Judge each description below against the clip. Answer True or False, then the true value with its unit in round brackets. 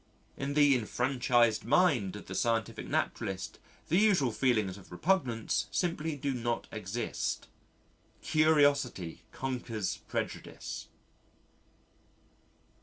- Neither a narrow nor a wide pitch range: True (4.7 semitones)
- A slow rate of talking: True (95 wpm)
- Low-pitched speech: True (125 Hz)